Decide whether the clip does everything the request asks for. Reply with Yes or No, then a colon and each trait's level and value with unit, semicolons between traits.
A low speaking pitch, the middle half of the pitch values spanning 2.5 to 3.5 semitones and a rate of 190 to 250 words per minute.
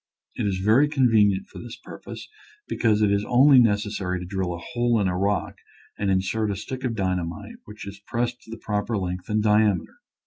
Yes: low, 105 Hz; average, 3.2 semitones; fast, 205 wpm